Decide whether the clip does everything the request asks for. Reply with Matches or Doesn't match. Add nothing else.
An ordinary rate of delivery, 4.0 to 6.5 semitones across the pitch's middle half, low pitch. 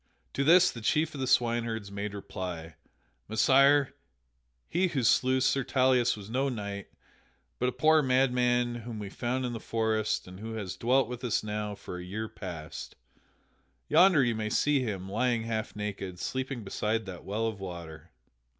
Matches